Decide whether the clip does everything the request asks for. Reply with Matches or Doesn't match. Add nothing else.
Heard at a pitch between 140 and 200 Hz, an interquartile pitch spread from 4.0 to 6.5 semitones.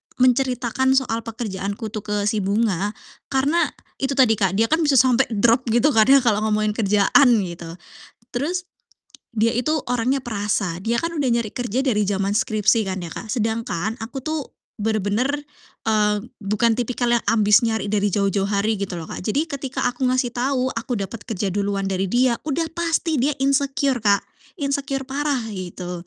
Doesn't match